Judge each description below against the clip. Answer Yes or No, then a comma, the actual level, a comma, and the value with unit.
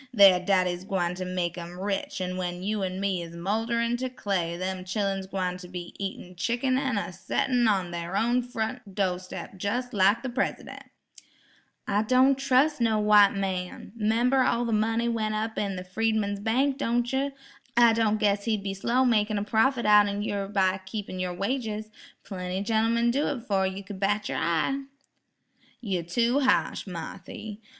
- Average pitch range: Yes, average, 3.9 semitones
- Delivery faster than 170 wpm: Yes, average, 180 wpm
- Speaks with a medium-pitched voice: No, high, 205 Hz